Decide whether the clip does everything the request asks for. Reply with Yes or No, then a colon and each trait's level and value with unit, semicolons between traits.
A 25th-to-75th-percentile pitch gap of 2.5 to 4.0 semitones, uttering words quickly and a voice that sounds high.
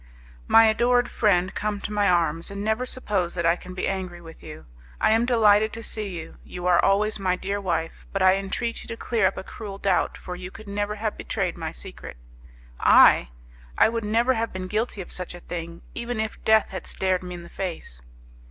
Yes: average, 3.4 semitones; fast, 215 wpm; high, 195 Hz